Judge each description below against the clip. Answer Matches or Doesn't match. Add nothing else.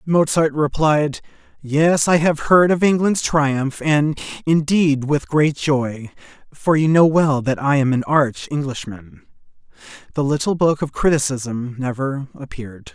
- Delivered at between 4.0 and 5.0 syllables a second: Doesn't match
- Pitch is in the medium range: Matches